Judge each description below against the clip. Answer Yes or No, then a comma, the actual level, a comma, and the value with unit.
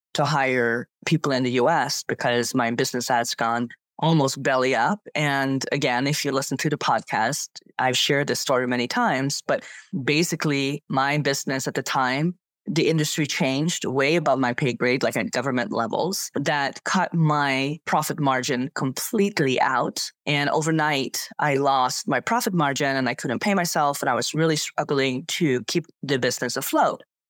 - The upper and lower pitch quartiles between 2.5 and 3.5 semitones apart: Yes, average, 2.8 semitones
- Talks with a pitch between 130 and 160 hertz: Yes, medium, 140 Hz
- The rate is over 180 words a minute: No, average, 165 wpm